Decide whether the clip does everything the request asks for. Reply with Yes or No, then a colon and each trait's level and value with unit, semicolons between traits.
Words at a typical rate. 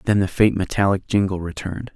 Yes: average, 185 wpm